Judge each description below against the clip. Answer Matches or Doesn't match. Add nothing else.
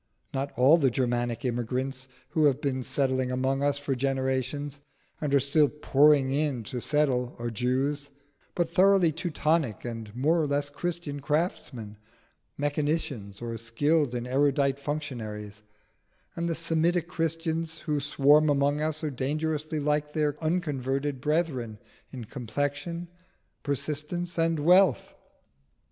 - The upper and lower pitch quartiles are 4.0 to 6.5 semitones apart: Doesn't match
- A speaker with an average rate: Doesn't match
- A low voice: Doesn't match